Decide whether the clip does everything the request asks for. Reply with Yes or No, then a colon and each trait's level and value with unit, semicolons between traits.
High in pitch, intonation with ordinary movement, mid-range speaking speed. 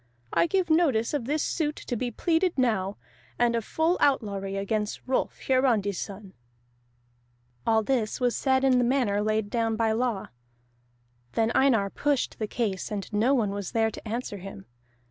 Yes: high, 230 Hz; average, 4.2 semitones; average, 165 wpm